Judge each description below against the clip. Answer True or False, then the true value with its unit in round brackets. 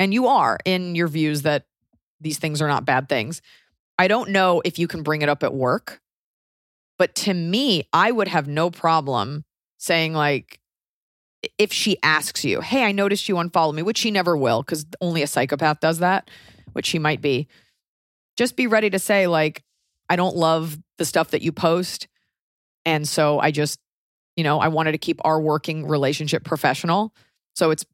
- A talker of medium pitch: True (160 Hz)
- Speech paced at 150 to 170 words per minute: False (190 wpm)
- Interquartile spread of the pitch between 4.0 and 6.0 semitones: False (3.2 semitones)